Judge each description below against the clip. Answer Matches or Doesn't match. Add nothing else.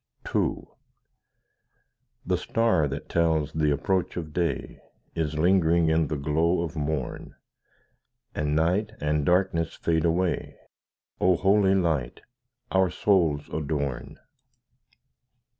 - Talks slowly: Matches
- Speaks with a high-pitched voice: Doesn't match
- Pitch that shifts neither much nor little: Matches